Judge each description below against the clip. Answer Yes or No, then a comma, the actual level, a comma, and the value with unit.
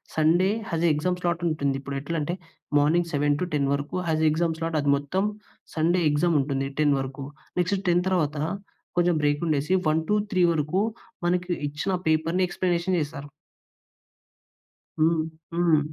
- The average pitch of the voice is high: No, medium, 160 Hz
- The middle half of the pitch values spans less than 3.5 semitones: Yes, average, 3.1 semitones